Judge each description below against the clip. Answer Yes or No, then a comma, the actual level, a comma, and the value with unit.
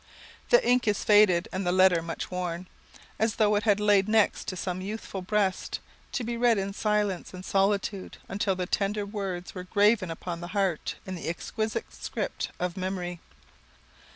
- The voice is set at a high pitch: Yes, high, 195 Hz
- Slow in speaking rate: No, average, 175 wpm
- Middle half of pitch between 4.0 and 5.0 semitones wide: No, narrow, 2.5 semitones